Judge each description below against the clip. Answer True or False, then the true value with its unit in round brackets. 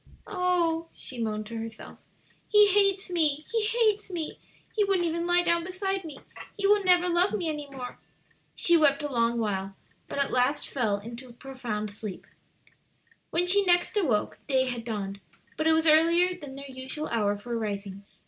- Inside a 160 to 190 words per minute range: True (180 wpm)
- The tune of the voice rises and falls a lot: True (7.4 semitones)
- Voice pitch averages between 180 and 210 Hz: False (300 Hz)